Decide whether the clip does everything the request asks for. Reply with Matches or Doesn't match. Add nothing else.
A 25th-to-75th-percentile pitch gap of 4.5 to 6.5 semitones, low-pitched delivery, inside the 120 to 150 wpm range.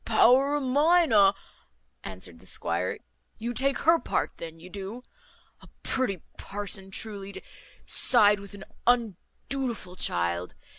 Doesn't match